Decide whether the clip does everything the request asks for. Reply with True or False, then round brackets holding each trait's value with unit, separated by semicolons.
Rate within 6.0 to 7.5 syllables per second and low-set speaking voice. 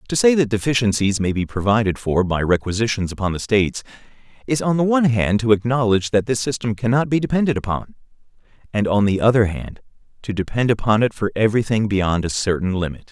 True (6.2 syllables/s; 110 Hz)